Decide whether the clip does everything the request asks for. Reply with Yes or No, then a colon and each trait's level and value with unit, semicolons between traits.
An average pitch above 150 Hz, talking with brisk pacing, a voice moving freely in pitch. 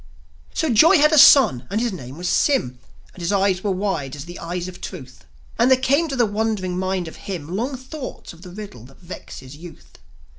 Yes: high, 190 Hz; fast, 215 wpm; wide, 6.3 semitones